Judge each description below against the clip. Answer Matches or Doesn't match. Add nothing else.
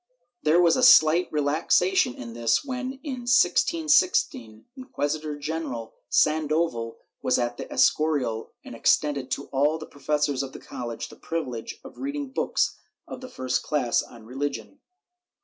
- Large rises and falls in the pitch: Matches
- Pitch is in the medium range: Matches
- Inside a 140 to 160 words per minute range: Matches